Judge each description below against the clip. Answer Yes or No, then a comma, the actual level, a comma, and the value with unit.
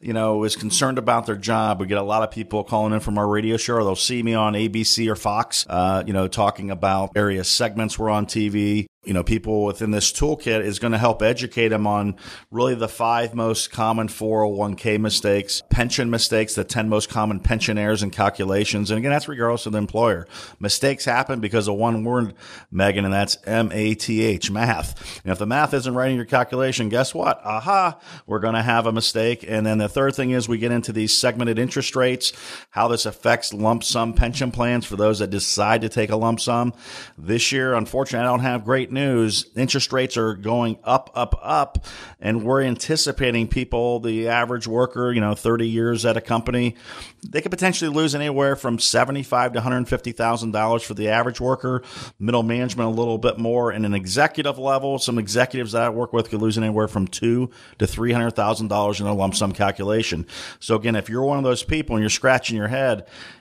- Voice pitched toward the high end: No, low, 115 Hz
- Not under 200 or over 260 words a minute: Yes, fast, 205 wpm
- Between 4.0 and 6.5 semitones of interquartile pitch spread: No, narrow, 2.5 semitones